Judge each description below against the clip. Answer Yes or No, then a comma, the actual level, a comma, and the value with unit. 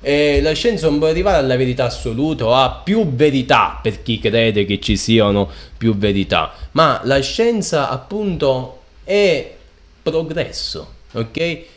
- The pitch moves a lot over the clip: Yes, wide, 6.0 semitones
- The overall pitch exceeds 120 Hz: Yes, low, 135 Hz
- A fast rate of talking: No, average, 145 wpm